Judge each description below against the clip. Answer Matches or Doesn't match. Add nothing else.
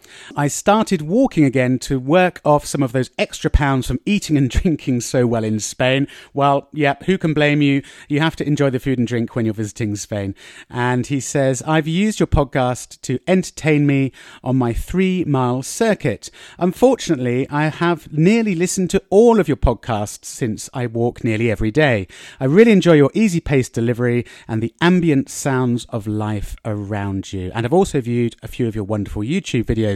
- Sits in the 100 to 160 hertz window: Matches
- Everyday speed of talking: Matches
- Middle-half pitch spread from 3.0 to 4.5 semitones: Doesn't match